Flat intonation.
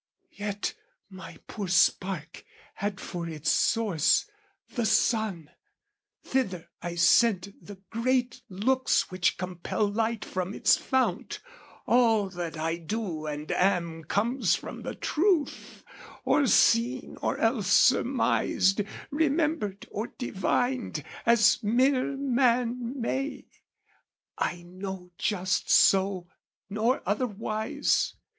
No: average, 5.1 semitones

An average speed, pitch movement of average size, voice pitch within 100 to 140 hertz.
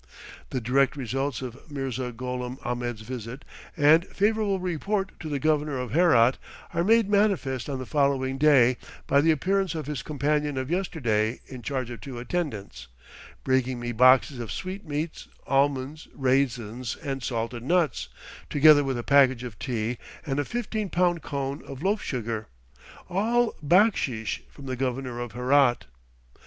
Yes: average, 150 wpm; average, 4.1 semitones; low, 135 Hz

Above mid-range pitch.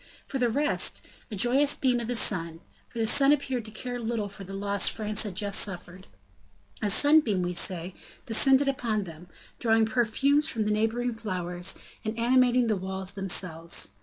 Yes: high, 220 Hz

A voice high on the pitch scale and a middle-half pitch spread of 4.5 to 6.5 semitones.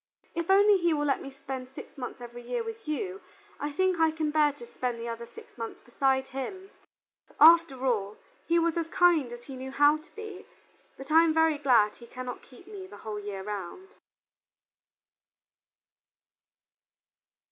Yes: very high, 290 Hz; wide, 5.4 semitones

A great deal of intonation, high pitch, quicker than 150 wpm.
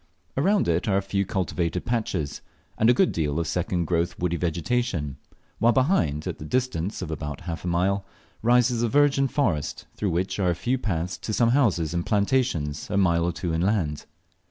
No: wide, 6.0 semitones; very low, 90 Hz; average, 190 wpm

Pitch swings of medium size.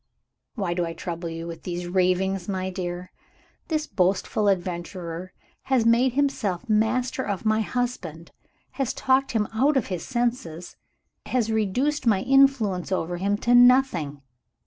No: wide, 5.8 semitones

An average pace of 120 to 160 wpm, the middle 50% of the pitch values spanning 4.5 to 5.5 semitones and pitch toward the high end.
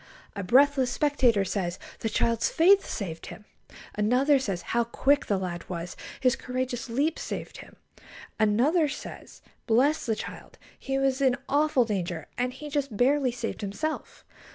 Yes: average, 155 wpm; average, 5.1 semitones; very high, 250 Hz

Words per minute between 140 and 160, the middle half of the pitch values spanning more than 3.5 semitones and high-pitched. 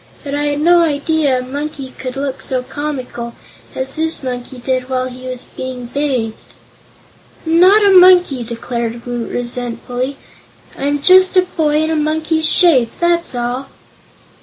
Yes: average, 155 wpm; average, 4.0 semitones; very high, 275 Hz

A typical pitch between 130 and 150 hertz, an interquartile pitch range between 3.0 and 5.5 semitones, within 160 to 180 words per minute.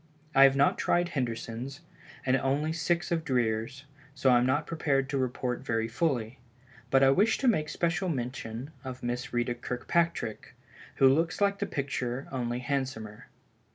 Yes: low, 135 Hz; average, 3.8 semitones; average, 170 wpm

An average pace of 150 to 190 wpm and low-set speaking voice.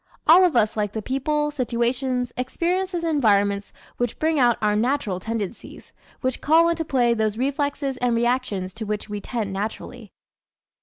No: average, 160 wpm; high, 245 Hz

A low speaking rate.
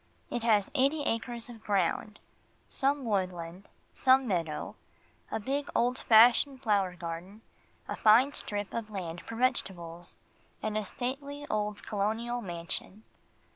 Yes: slow, 130 wpm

